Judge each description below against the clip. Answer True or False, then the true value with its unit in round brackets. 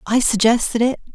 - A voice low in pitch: False (235 Hz)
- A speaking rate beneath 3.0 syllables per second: False (5.5 syllables/s)